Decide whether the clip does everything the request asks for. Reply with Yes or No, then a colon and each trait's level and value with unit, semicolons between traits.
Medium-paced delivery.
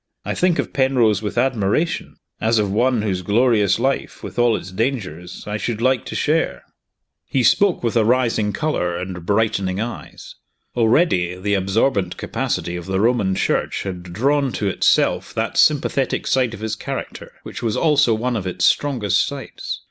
Yes: average, 170 wpm